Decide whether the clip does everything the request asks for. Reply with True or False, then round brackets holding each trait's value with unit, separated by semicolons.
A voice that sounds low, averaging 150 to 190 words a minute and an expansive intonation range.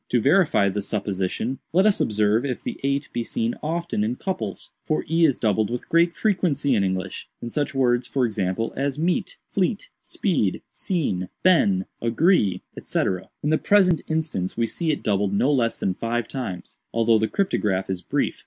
True (120 Hz; 170 wpm; 7.4 semitones)